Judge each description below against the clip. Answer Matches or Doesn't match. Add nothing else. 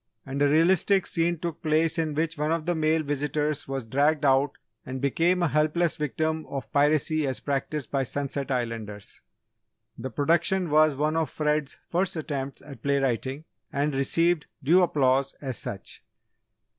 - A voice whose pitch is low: Doesn't match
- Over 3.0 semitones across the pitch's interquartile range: Doesn't match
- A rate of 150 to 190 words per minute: Matches